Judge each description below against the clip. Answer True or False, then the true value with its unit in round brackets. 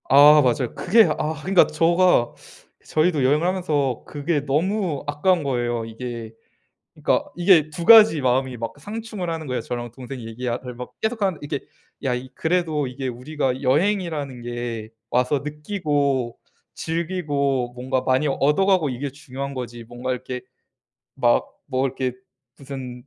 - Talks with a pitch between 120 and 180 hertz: True (140 Hz)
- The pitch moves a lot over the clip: False (4.5 semitones)